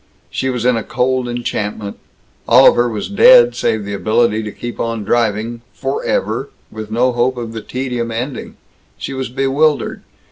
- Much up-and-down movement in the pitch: No, average, 2.8 semitones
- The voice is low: Yes, low, 120 Hz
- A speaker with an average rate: Yes, average, 170 wpm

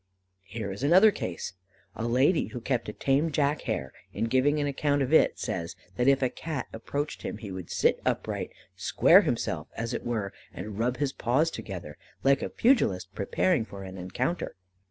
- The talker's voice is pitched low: Yes, low, 125 Hz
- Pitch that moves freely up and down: Yes, wide, 6.5 semitones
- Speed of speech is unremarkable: Yes, average, 185 wpm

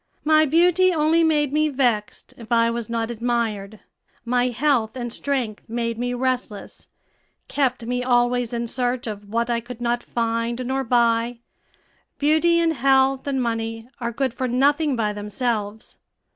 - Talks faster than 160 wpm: No, average, 155 wpm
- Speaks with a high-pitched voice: Yes, high, 245 Hz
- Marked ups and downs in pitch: No, average, 2.7 semitones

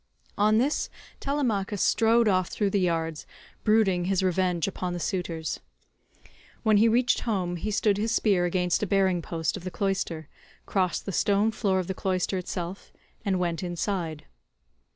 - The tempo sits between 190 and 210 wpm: No, average, 160 wpm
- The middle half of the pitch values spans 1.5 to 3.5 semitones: Yes, average, 2.9 semitones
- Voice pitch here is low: No, high, 190 Hz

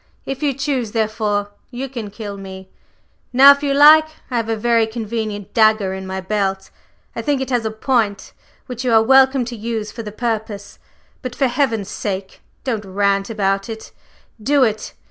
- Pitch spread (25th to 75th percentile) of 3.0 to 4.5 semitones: Yes, average, 3.7 semitones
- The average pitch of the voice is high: Yes, high, 225 Hz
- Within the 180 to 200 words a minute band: Yes, average, 185 wpm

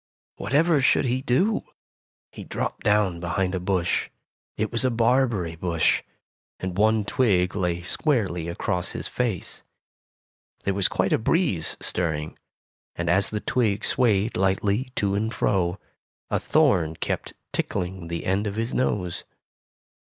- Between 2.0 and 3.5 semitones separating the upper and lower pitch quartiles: No, average, 4.5 semitones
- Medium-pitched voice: No, low, 100 Hz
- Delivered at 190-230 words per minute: No, average, 140 wpm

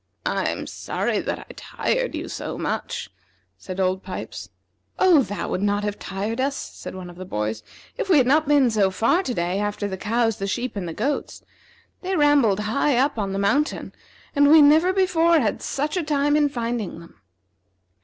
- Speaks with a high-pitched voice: Yes, high, 235 Hz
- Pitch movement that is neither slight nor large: No, wide, 6.9 semitones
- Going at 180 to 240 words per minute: Yes, average, 195 wpm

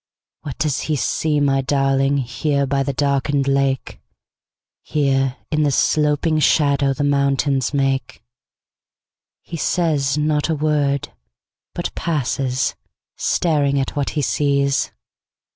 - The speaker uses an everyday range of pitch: No, narrow, 1.5 semitones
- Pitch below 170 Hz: Yes, medium, 140 Hz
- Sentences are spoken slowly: Yes, slow, 100 wpm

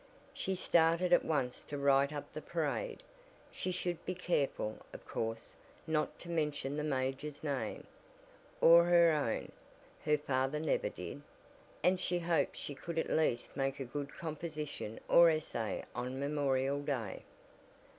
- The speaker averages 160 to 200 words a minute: No, average, 145 wpm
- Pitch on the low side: No, medium, 150 Hz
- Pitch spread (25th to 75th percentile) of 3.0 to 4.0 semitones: Yes, average, 3.6 semitones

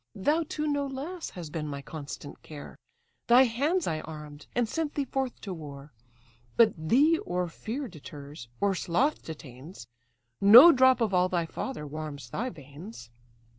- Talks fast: No, average, 160 wpm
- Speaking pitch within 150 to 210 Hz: Yes, medium, 185 Hz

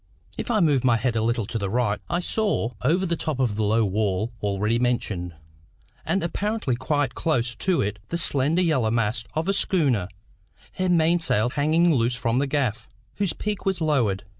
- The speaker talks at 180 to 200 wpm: Yes, average, 190 wpm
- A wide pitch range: Yes, wide, 7.0 semitones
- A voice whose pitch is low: Yes, low, 125 Hz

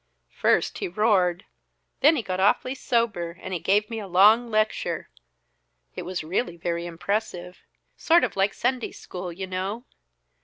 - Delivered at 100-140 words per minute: No, average, 155 wpm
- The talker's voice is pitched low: No, high, 195 Hz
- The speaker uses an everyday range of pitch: Yes, average, 4.0 semitones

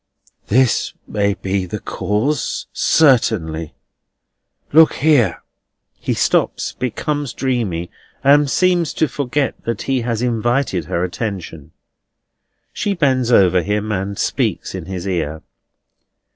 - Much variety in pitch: Yes, wide, 6.4 semitones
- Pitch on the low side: Yes, low, 115 Hz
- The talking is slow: Yes, slow, 115 wpm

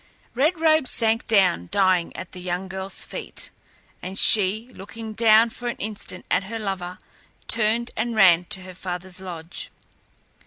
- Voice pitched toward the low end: No, high, 195 Hz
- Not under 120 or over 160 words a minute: Yes, average, 155 wpm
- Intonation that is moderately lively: Yes, average, 3.6 semitones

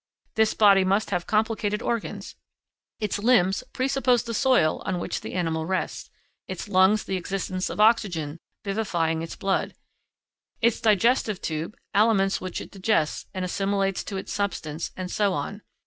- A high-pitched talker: Yes, high, 195 Hz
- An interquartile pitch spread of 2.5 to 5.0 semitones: Yes, average, 3.0 semitones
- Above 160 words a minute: No, average, 150 wpm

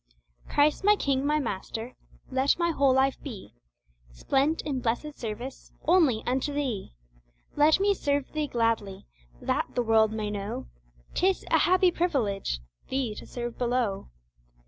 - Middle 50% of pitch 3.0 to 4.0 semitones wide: No, average, 5.0 semitones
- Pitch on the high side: Yes, very high, 260 Hz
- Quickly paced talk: No, average, 145 wpm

